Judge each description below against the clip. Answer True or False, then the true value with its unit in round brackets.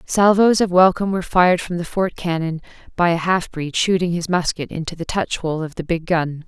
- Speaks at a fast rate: True (220 wpm)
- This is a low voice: False (175 Hz)